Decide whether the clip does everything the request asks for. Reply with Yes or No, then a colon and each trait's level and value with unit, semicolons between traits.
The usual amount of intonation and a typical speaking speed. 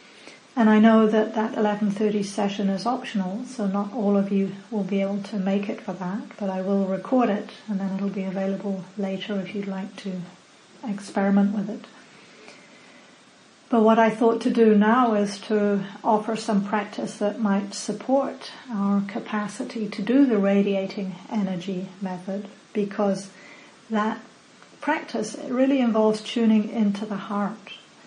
No: narrow, 2.0 semitones; average, 155 wpm